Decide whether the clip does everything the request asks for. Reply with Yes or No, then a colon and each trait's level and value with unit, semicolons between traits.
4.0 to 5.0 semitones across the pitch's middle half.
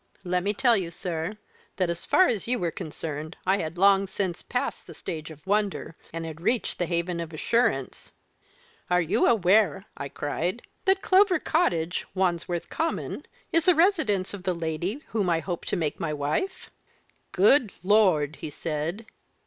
Yes: average, 4.7 semitones